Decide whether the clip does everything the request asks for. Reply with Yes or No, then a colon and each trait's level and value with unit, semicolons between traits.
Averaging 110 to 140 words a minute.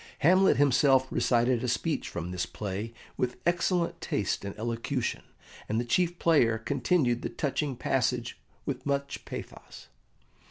Yes: slow, 135 wpm